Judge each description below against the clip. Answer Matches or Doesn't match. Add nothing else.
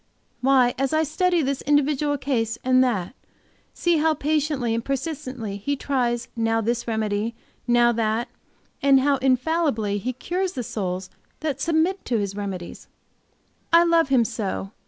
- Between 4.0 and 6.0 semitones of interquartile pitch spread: Matches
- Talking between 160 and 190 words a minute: Doesn't match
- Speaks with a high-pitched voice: Matches